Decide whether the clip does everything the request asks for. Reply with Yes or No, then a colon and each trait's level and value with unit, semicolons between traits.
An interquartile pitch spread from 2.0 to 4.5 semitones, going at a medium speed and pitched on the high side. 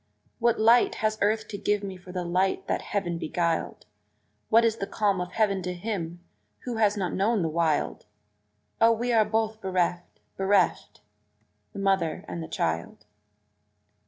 Yes: average, 3.7 semitones; average, 160 wpm; high, 195 Hz